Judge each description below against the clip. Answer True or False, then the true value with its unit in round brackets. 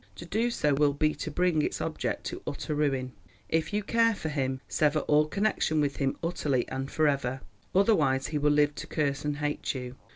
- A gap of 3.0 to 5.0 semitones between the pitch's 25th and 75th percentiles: False (2.6 semitones)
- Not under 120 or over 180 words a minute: False (205 wpm)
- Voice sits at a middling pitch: True (150 Hz)